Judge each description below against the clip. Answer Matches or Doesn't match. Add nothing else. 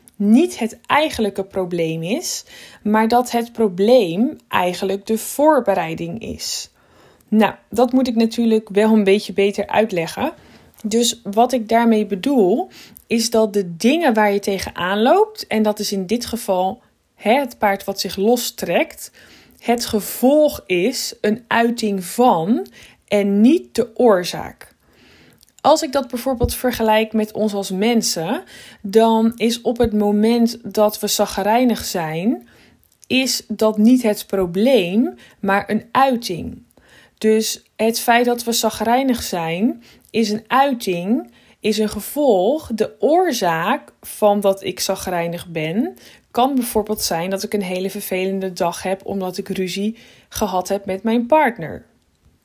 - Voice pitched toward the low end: Doesn't match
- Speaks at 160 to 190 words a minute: Doesn't match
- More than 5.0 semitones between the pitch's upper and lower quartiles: Doesn't match